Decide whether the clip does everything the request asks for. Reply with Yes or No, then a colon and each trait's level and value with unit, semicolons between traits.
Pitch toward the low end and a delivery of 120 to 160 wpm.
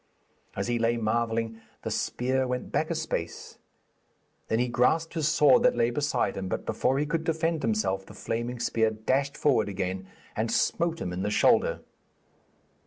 No: low, 120 Hz; average, 175 wpm